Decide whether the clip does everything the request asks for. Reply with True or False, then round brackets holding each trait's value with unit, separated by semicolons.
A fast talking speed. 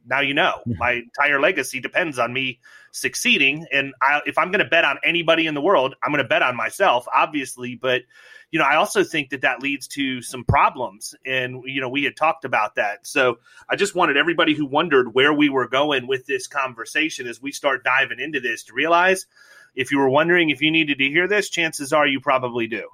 True (225 wpm)